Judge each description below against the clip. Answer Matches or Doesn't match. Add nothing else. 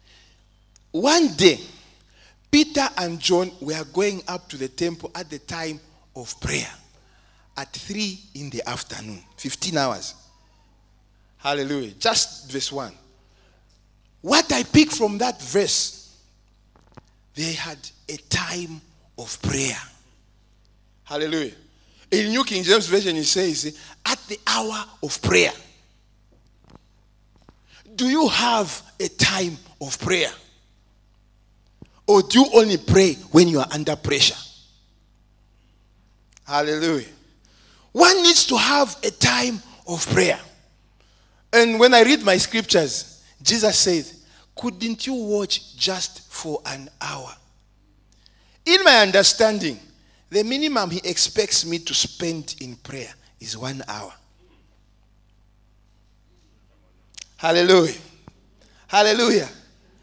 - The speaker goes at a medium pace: Doesn't match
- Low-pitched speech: Doesn't match